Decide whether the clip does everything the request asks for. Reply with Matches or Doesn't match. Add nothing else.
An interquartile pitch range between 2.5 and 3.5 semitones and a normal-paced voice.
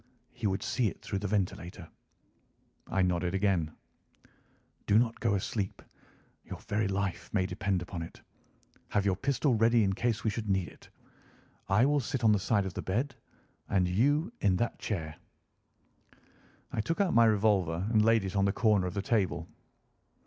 Matches